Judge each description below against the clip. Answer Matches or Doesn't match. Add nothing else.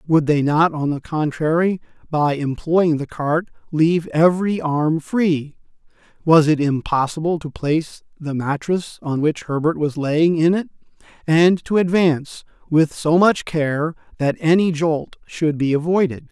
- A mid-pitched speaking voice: Matches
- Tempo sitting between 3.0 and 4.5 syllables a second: Matches